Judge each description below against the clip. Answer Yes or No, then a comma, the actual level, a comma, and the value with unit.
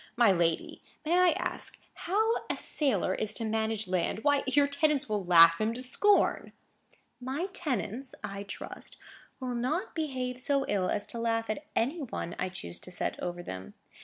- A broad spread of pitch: Yes, wide, 6.3 semitones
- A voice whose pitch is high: Yes, high, 235 Hz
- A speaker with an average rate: Yes, average, 175 wpm